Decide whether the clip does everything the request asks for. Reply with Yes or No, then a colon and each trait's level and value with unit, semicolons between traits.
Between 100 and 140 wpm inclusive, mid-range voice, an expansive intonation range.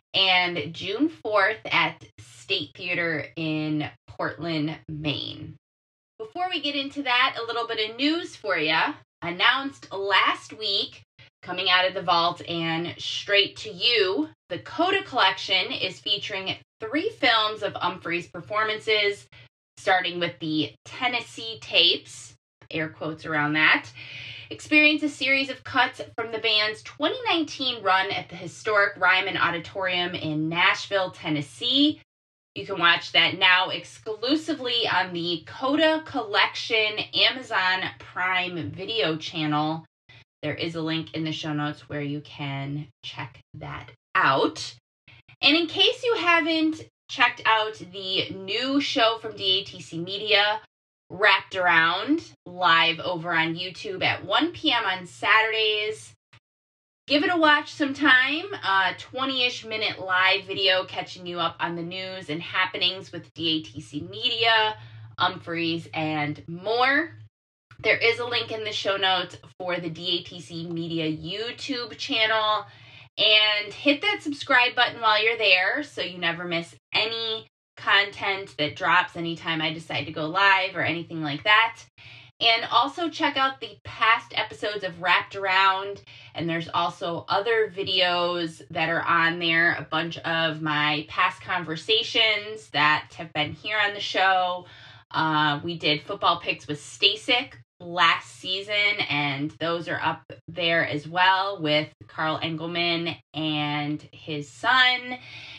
Yes: slow, 135 wpm; medium, 180 Hz; wide, 6.0 semitones